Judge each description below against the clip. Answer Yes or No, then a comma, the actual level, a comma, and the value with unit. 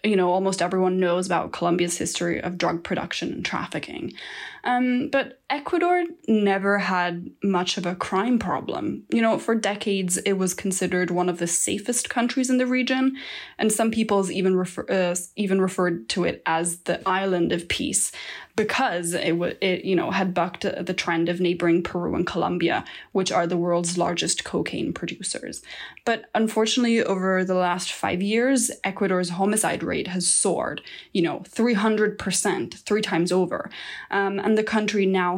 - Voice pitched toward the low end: No, high, 190 Hz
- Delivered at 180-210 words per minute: No, average, 165 wpm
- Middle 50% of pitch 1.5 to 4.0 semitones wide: Yes, average, 3.6 semitones